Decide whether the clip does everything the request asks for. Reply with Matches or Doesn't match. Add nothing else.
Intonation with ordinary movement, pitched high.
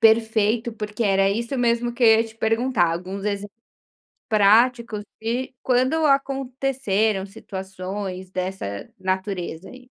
Matches